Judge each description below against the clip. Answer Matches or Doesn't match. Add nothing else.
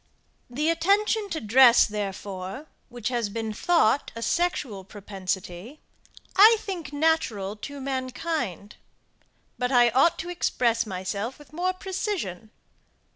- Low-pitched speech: Doesn't match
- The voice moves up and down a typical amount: Doesn't match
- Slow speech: Matches